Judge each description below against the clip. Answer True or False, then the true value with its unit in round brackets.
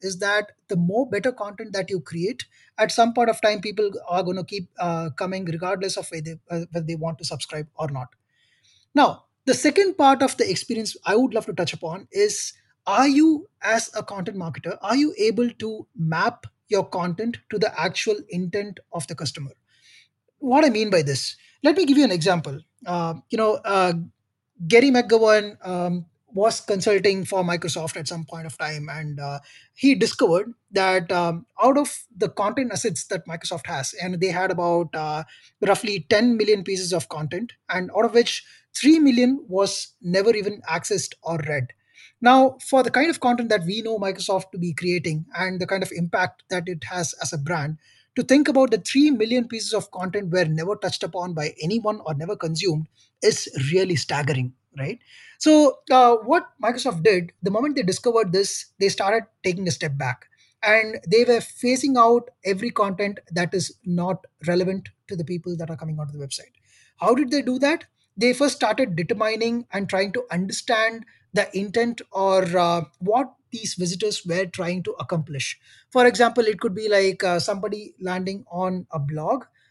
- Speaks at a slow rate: False (185 wpm)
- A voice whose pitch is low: False (195 Hz)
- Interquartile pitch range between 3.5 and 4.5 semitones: False (5.0 semitones)